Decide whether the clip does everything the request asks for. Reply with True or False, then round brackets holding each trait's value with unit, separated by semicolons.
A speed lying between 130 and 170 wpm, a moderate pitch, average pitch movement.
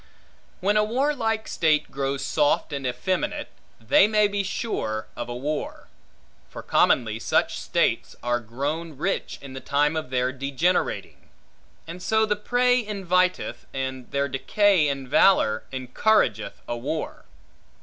False (140 wpm; 150 Hz; 7.5 semitones)